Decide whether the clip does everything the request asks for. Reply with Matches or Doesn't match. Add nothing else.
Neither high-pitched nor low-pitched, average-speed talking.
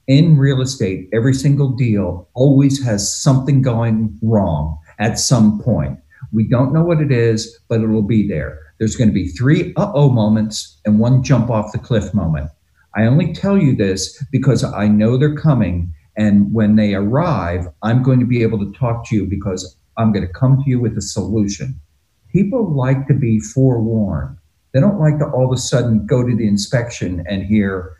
Doesn't match